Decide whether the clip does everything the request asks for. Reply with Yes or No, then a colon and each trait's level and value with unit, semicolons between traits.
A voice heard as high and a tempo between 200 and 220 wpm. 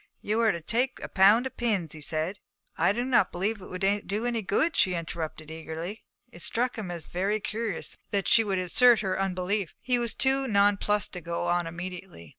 Yes: high, 195 Hz; fast, 205 wpm